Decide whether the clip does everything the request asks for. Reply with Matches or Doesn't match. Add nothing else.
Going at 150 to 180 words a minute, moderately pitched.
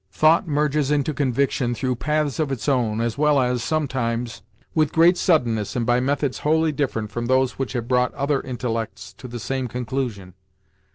Doesn't match